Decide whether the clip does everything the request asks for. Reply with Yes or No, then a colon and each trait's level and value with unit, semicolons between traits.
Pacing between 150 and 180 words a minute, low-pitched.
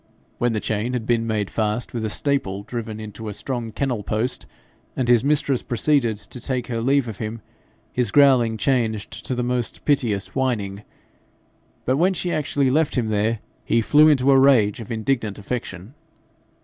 Yes: average, 175 wpm; low, 120 Hz